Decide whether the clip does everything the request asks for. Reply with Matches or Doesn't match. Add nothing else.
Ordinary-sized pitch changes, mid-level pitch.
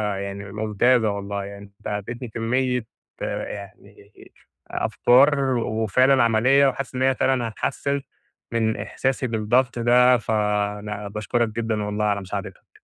Doesn't match